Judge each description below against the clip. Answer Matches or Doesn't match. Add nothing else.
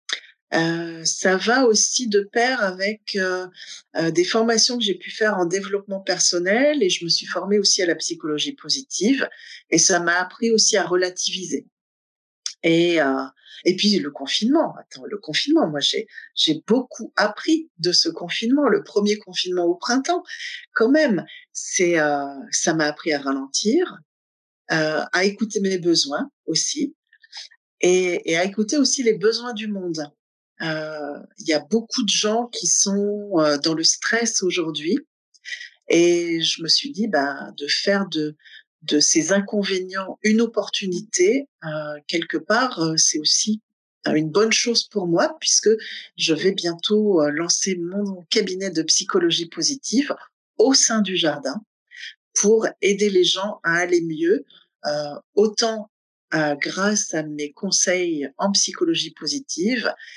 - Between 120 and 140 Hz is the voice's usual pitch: Doesn't match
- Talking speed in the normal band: Matches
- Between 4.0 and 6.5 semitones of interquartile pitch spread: Matches